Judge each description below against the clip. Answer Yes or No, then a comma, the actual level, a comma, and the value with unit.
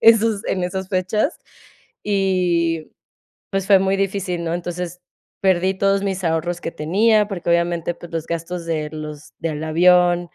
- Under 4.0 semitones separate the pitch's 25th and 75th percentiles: Yes, narrow, 2.5 semitones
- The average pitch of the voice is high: No, medium, 180 Hz